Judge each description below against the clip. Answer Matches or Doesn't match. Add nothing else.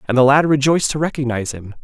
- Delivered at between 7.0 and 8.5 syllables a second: Matches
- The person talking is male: Matches